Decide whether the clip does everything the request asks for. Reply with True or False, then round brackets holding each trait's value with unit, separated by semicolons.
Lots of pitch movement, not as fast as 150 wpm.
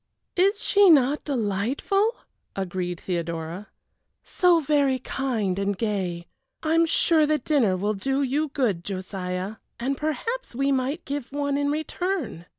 True (7.7 semitones; 140 wpm)